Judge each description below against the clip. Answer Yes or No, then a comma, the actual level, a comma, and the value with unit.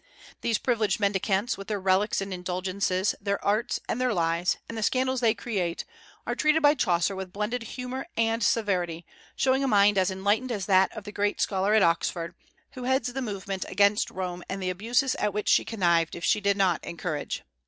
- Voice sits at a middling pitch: No, high, 200 Hz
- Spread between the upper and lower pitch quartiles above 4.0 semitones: No, average, 3.6 semitones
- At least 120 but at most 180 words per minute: No, average, 195 wpm